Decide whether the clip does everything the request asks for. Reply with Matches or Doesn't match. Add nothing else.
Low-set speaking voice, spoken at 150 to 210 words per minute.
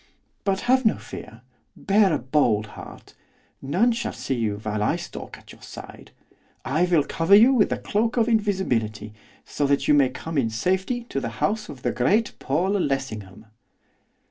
Doesn't match